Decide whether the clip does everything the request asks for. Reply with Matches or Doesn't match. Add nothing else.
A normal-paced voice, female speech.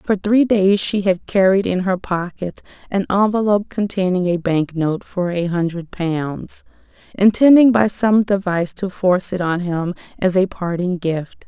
Matches